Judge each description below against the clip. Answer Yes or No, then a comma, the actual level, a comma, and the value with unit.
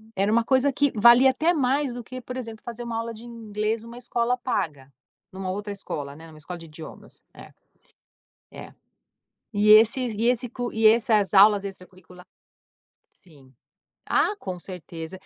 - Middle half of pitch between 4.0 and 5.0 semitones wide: Yes, average, 4.6 semitones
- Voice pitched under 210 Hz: No, high, 220 Hz